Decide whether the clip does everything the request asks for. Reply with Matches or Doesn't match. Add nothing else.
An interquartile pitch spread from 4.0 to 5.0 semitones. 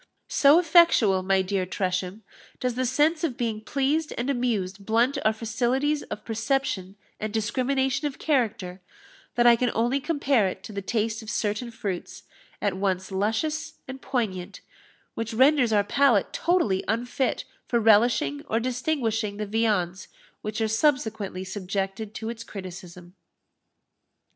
Matches